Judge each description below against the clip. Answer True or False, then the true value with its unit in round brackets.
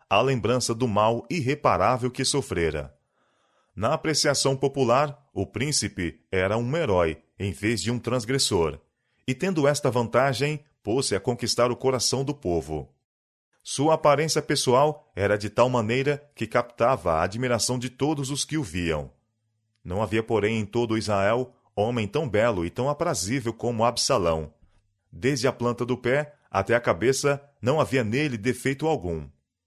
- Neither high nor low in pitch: False (120 Hz)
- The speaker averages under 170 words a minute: True (150 wpm)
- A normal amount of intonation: True (5.0 semitones)